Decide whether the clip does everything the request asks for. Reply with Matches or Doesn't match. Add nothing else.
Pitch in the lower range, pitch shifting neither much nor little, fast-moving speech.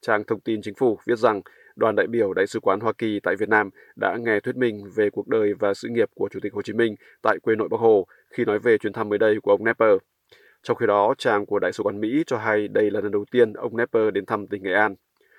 Matches